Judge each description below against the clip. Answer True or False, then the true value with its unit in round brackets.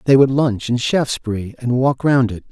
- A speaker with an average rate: False (215 wpm)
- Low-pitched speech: True (125 Hz)